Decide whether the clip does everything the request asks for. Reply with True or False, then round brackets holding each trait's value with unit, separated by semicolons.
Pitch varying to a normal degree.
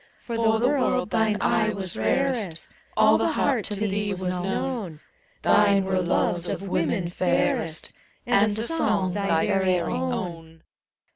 True (3.7 semitones)